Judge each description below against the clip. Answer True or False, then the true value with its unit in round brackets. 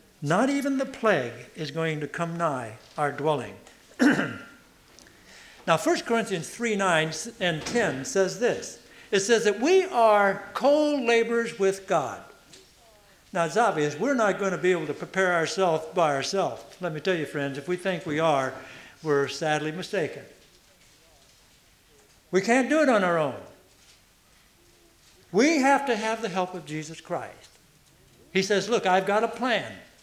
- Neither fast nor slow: True (160 wpm)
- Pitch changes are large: True (6.5 semitones)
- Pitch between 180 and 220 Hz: True (185 Hz)